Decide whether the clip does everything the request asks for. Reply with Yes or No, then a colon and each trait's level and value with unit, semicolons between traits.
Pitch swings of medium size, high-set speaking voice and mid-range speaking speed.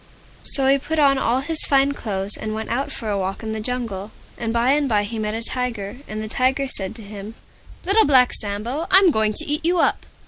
No: average, 4.4 semitones; high, 235 Hz; fast, 235 wpm